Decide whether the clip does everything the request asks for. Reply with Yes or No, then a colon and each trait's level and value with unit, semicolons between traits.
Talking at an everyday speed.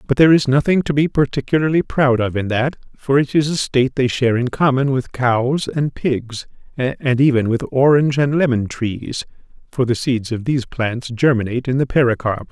Yes: average, 195 wpm